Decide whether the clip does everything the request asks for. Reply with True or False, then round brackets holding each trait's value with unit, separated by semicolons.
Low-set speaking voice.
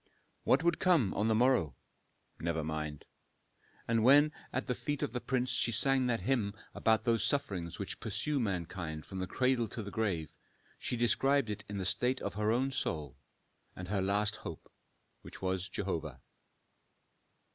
True (110 Hz)